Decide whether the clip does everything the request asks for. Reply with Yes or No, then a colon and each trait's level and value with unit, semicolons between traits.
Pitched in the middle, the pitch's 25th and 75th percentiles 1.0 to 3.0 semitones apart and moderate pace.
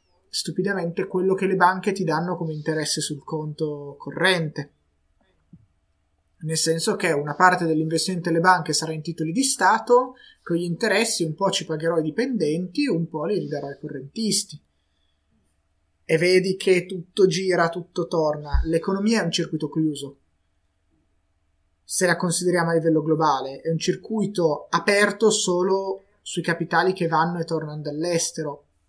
No: medium, 165 Hz; average, 3.8 semitones; average, 145 wpm